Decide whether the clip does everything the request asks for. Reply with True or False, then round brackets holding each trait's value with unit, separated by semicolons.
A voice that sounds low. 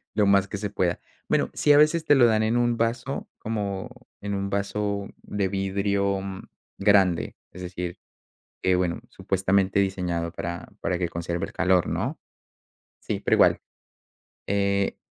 True (100 Hz)